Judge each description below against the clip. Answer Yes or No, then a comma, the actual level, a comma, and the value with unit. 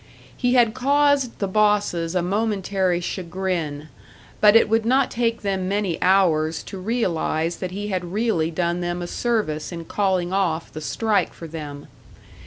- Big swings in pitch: No, average, 4.2 semitones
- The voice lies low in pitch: No, high, 190 Hz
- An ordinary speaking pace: Yes, average, 160 wpm